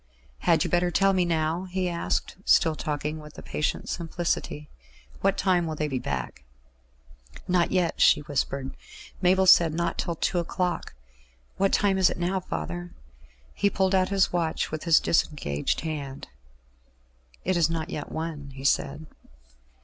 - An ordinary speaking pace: Yes, average, 155 wpm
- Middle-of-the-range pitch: Yes, medium, 165 Hz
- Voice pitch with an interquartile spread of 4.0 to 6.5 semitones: No, average, 3.3 semitones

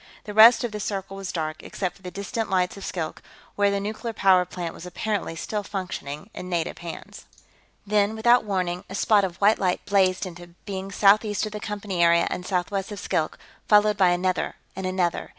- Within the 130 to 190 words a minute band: No, average, 200 wpm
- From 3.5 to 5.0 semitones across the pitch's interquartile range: No, narrow, 2.5 semitones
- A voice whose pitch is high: Yes, high, 195 Hz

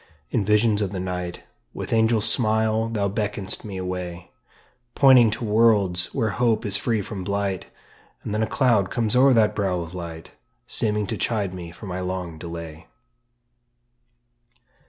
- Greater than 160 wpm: No, average, 155 wpm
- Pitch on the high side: No, low, 100 Hz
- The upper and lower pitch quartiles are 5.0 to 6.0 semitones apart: No, average, 3.3 semitones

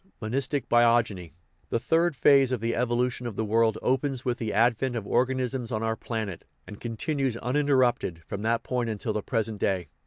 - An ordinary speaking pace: Yes, average, 185 wpm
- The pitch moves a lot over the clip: No, average, 2.7 semitones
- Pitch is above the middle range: No, low, 120 Hz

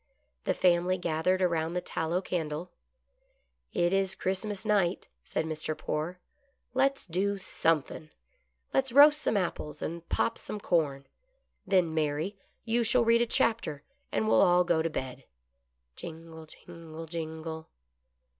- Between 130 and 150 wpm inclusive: Yes, average, 145 wpm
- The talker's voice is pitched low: No, medium, 175 Hz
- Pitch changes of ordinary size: Yes, average, 4.0 semitones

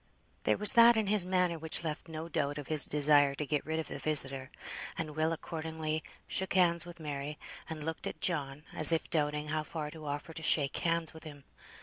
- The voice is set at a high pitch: No, medium, 155 Hz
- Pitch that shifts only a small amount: Yes, narrow, 1.9 semitones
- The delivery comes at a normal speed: No, fast, 215 wpm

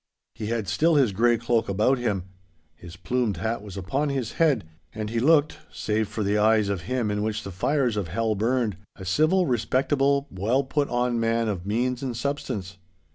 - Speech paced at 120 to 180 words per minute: No, average, 190 wpm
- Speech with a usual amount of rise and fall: Yes, average, 4.0 semitones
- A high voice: No, low, 115 Hz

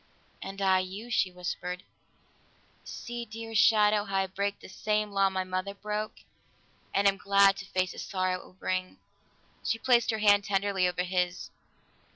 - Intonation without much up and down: Yes, narrow, 2.2 semitones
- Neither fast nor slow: Yes, average, 170 wpm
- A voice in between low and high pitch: No, high, 195 Hz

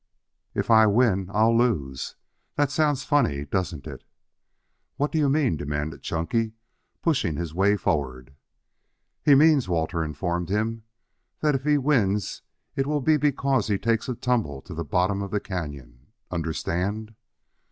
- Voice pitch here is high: No, low, 105 Hz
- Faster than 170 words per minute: No, average, 150 wpm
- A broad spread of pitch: Yes, wide, 8.4 semitones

